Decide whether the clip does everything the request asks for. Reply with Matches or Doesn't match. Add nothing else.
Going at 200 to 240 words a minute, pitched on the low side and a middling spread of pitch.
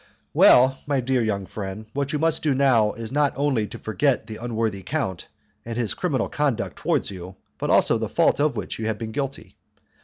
Matches